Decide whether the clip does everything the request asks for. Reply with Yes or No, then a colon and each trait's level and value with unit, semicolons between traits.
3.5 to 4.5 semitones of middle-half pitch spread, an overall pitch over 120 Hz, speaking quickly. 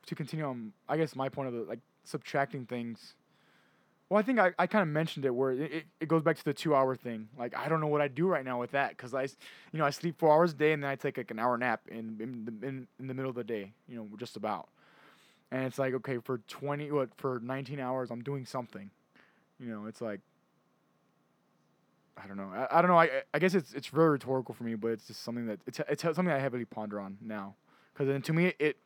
Yes: average, 4.2 semitones; low, 135 Hz; fast, 260 wpm